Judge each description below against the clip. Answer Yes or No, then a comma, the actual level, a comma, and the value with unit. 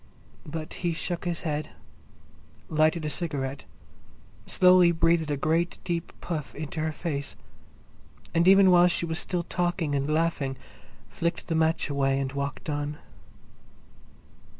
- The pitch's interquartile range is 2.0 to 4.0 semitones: Yes, average, 2.8 semitones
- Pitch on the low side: No, medium, 160 Hz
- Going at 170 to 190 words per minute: No, slow, 135 wpm